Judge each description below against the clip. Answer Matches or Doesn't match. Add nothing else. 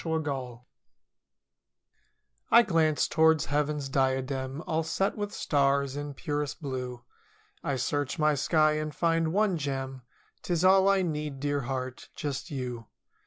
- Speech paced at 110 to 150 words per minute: Matches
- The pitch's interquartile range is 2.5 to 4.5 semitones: Matches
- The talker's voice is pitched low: Doesn't match